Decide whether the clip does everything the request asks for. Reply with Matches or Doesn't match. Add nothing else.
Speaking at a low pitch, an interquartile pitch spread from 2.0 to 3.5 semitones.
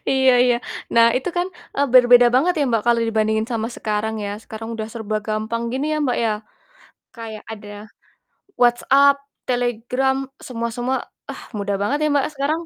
Doesn't match